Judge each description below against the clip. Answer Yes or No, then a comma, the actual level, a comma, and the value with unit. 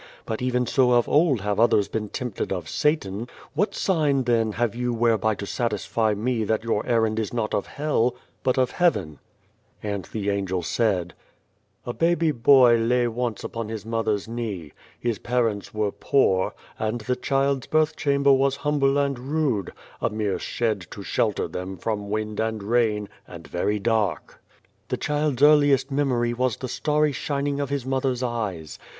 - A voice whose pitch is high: No, low, 120 Hz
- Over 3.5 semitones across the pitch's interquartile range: Yes, average, 4.3 semitones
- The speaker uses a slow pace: No, average, 175 wpm